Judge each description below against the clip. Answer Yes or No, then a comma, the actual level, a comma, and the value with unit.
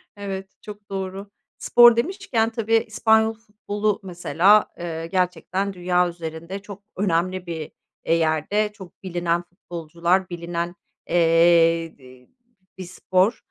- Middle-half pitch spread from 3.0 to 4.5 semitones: Yes, average, 3.4 semitones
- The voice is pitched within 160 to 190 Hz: Yes, medium, 185 Hz